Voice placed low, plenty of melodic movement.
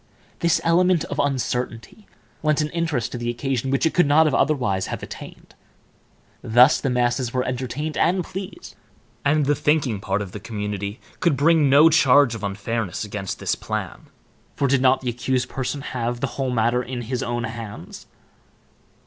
No: low, 130 Hz; average, 4.2 semitones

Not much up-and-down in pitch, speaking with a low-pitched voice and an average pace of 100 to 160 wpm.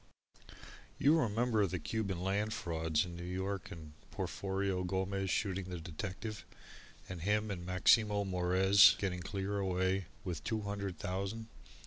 Yes: narrow, 2.1 semitones; very low, 95 Hz; slow, 135 wpm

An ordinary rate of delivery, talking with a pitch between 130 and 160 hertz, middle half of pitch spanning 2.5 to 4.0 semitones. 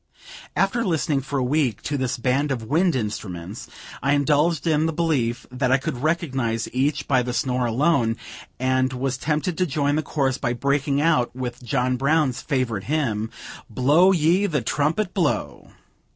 Yes: average, 165 wpm; medium, 140 Hz; average, 3.7 semitones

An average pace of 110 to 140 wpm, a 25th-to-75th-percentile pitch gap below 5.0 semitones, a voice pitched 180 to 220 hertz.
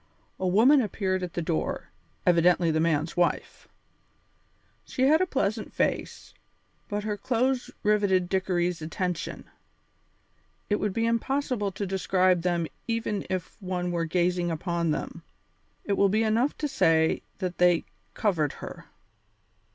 Yes: slow, 135 wpm; average, 3.7 semitones; medium, 185 Hz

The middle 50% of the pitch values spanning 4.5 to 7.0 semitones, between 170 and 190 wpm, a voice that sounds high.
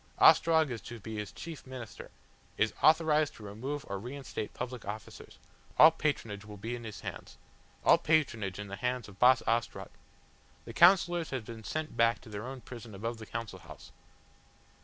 No: average, 5.0 semitones; average, 180 wpm; low, 120 Hz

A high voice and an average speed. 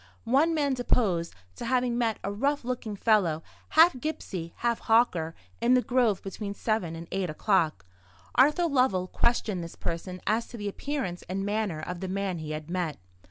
Yes: high, 205 Hz; average, 175 wpm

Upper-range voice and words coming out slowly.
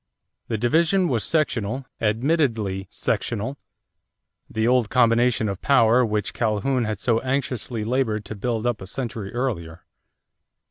No: low, 115 Hz; slow, 130 wpm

